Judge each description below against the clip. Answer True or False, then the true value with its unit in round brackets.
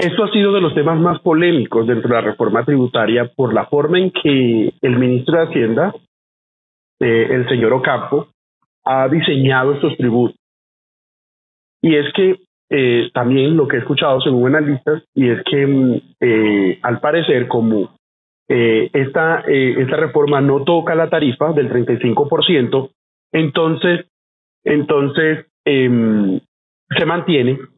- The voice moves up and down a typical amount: True (4.8 semitones)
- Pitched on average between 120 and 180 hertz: True (135 Hz)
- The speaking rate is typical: True (140 wpm)